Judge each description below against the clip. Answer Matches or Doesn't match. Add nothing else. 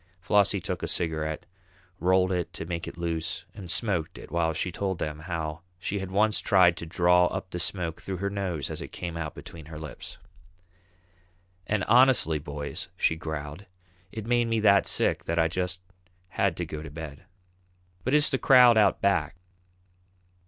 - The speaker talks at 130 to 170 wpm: Doesn't match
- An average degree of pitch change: Matches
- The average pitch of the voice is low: Matches